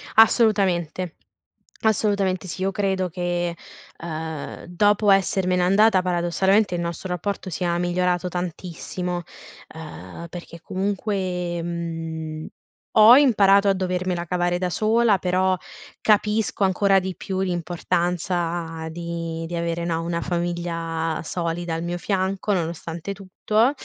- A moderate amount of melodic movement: No, narrow, 2.3 semitones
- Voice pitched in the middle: Yes, medium, 180 Hz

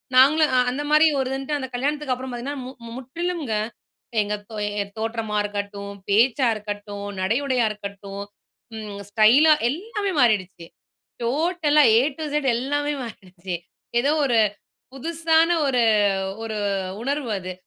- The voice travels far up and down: Yes, wide, 5.8 semitones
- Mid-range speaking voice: No, very high, 250 Hz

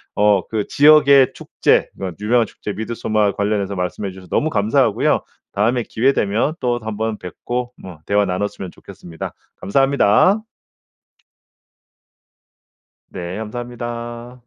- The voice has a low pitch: Yes, low, 110 Hz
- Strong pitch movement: No, average, 3.3 semitones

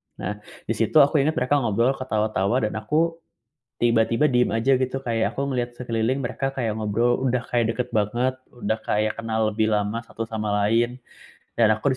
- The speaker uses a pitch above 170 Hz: No, low, 115 Hz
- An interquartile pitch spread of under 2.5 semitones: No, average, 2.8 semitones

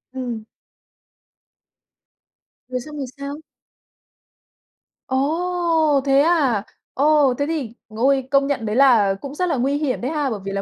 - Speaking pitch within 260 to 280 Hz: Yes, very high, 275 Hz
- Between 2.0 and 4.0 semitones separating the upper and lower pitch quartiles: Yes, average, 3.3 semitones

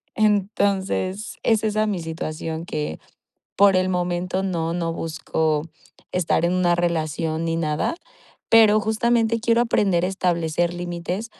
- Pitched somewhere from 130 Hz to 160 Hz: No, medium, 180 Hz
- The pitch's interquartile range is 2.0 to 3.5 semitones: No, average, 3.9 semitones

